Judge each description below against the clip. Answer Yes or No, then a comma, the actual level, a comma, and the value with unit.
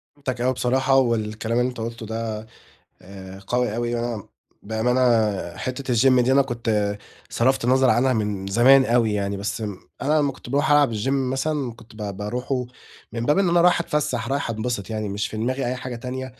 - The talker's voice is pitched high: No, low, 120 Hz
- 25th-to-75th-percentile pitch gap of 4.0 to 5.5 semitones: No, average, 3.1 semitones